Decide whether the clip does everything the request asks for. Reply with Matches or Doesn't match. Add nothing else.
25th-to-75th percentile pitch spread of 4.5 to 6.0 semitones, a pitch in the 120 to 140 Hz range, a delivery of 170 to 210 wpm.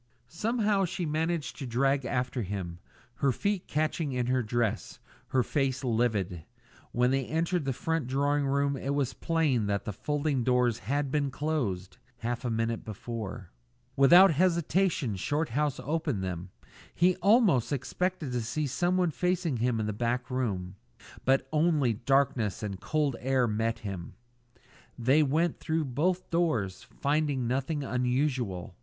Doesn't match